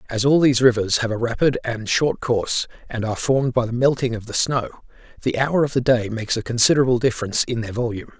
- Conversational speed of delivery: No, fast, 225 wpm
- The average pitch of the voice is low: Yes, low, 120 Hz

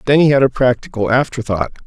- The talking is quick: No, average, 195 wpm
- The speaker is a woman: No, male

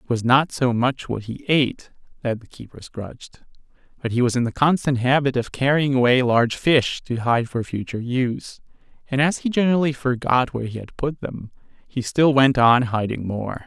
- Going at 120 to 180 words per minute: No, average, 200 wpm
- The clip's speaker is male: Yes, male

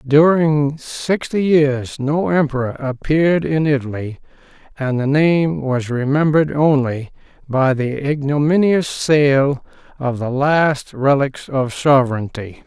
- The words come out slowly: Yes, slow, 115 wpm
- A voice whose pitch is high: No, medium, 140 Hz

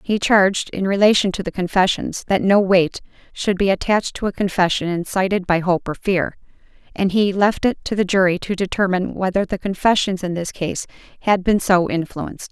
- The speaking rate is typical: Yes, average, 190 wpm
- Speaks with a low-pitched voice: No, high, 190 Hz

